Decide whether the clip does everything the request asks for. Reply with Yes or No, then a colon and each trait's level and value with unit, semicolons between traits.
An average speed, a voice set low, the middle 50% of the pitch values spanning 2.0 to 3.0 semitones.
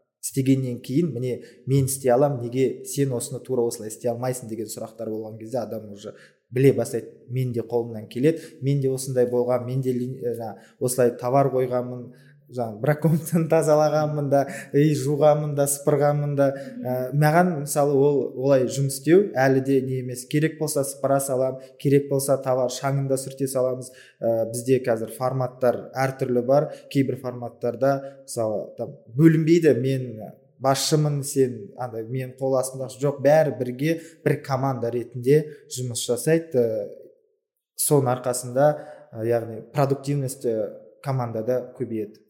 Yes: average, 135 wpm; low, 130 Hz; narrow, 2.6 semitones